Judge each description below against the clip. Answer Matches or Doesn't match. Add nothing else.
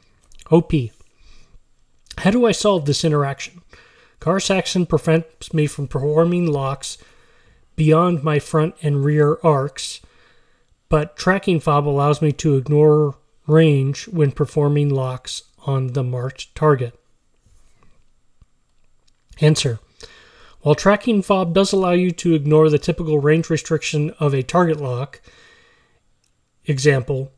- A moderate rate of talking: Doesn't match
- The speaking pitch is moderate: Matches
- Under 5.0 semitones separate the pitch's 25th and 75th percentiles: Matches